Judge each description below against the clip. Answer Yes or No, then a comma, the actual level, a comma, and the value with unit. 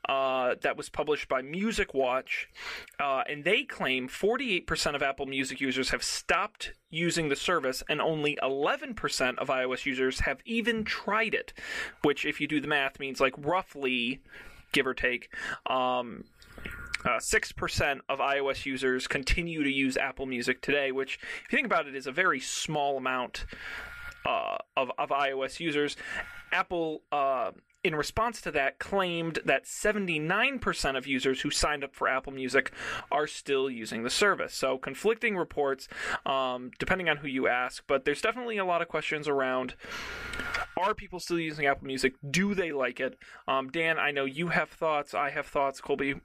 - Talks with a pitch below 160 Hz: Yes, medium, 140 Hz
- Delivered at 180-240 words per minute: No, average, 170 wpm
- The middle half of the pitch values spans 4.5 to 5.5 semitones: No, average, 4.1 semitones